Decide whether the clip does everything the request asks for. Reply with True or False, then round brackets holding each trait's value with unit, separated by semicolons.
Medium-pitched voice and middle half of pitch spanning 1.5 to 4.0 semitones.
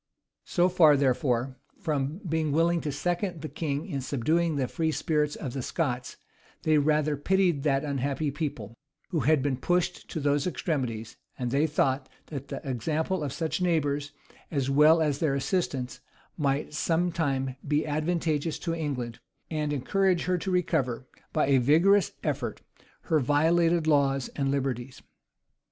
True (150 Hz; 3.1 semitones)